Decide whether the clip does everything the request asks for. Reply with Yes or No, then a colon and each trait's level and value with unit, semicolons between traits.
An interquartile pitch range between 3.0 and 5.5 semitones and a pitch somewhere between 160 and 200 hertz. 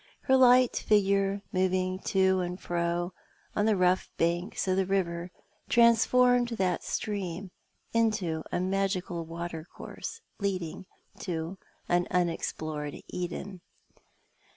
No: narrow, 2.5 semitones; medium, 185 Hz